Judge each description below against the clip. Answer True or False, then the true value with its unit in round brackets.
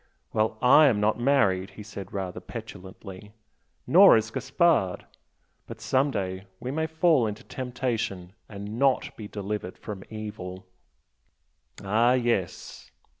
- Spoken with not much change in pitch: False (4.5 semitones)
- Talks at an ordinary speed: False (125 wpm)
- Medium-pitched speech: False (110 Hz)